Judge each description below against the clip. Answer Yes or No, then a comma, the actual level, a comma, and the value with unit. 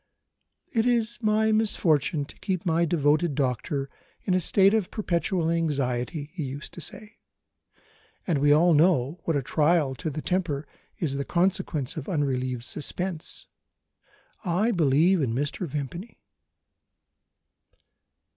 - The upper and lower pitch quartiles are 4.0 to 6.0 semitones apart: Yes, average, 4.7 semitones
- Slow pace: Yes, slow, 130 wpm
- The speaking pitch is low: No, medium, 160 Hz